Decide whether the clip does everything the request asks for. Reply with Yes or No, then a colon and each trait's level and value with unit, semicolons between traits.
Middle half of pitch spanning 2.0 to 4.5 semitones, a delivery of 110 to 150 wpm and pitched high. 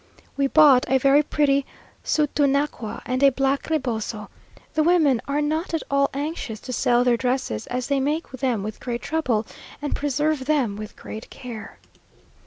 No: average, 3.3 semitones; average, 165 wpm; very high, 275 Hz